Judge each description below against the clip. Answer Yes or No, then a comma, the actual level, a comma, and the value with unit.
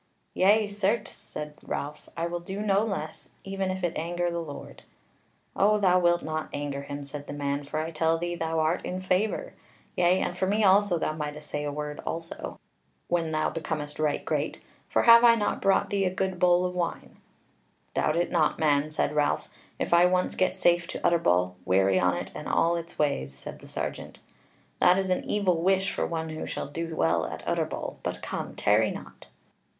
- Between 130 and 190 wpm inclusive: No, average, 200 wpm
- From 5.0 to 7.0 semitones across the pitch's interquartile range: No, average, 3.7 semitones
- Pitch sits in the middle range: Yes, medium, 170 Hz